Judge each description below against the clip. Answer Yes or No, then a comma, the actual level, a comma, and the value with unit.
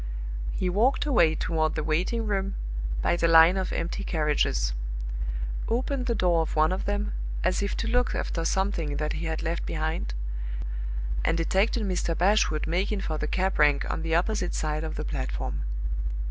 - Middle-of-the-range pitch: Yes, medium, 170 Hz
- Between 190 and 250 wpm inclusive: No, average, 175 wpm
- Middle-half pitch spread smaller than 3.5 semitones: No, average, 4.2 semitones